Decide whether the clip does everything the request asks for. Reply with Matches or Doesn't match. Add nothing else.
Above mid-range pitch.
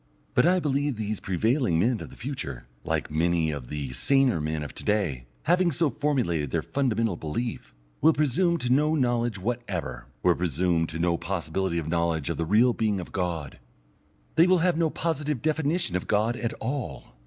Doesn't match